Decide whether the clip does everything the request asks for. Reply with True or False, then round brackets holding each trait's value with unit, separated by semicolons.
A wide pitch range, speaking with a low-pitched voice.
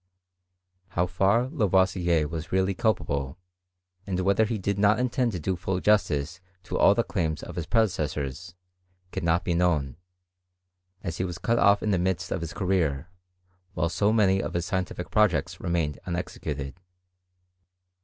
False (3.2 semitones; 90 Hz)